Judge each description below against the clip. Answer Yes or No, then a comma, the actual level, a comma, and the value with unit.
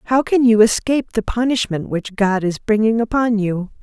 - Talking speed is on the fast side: No, average, 190 wpm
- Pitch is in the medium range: No, high, 220 Hz